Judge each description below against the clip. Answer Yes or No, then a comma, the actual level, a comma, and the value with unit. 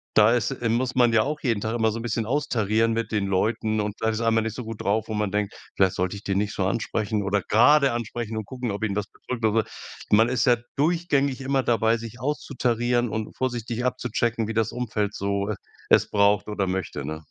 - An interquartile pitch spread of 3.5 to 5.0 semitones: No, narrow, 2.6 semitones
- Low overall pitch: Yes, low, 110 Hz